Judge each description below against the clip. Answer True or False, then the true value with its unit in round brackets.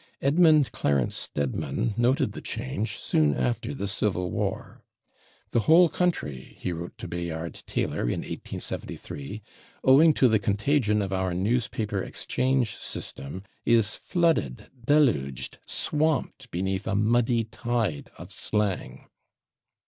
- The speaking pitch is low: True (105 Hz)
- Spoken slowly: True (120 wpm)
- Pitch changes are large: True (6.6 semitones)